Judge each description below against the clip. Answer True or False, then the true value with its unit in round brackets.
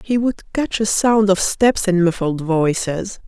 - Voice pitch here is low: False (195 Hz)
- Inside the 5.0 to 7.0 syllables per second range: False (3.8 syllables/s)